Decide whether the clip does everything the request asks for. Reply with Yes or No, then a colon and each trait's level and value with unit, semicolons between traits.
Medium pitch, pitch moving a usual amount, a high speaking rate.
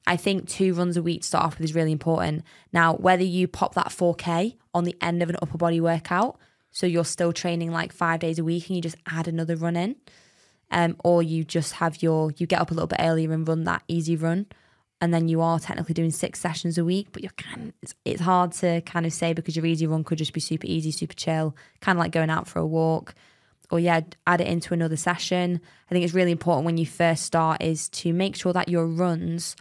No: medium, 170 Hz; narrow, 1.2 semitones; fast, 250 wpm